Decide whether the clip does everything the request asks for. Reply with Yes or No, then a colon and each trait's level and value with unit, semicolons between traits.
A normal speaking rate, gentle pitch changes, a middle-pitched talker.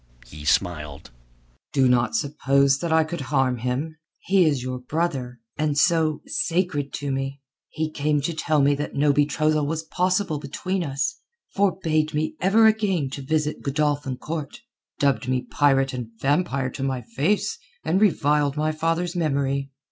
No: average, 155 wpm; average, 3.1 semitones; medium, 145 Hz